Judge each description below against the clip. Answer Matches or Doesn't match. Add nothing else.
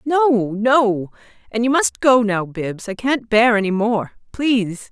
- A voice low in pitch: Doesn't match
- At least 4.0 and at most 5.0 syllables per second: Doesn't match